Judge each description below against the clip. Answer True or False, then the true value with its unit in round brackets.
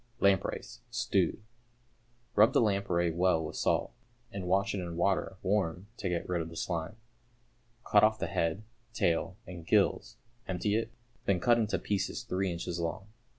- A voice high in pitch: False (95 Hz)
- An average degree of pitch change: True (3.1 semitones)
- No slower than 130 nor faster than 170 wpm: True (160 wpm)